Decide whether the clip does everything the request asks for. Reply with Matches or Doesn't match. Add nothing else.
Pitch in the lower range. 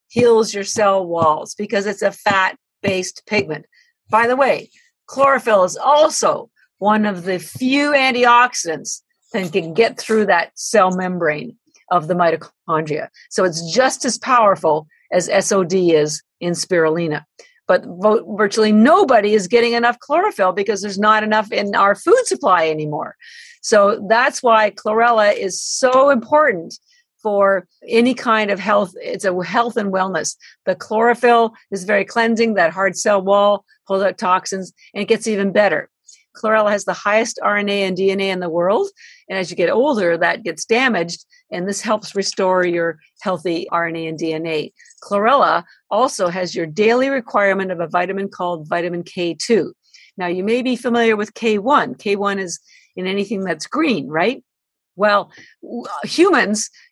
Doesn't match